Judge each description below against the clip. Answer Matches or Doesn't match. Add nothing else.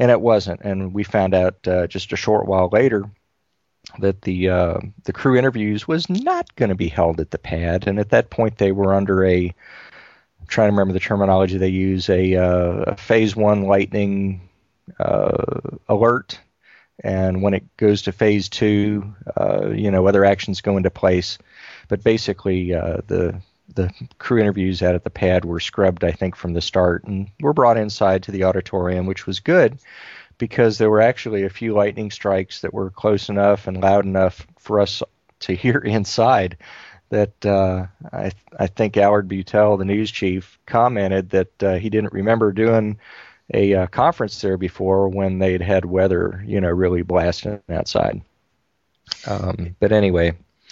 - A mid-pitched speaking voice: Doesn't match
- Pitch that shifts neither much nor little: Doesn't match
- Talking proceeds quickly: Doesn't match